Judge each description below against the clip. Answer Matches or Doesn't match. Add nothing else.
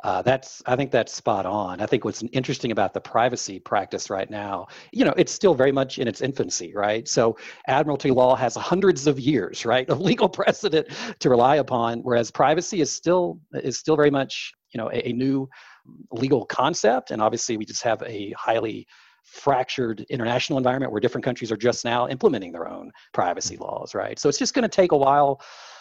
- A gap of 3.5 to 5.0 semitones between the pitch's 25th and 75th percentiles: Matches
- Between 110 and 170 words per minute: Doesn't match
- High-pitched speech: Doesn't match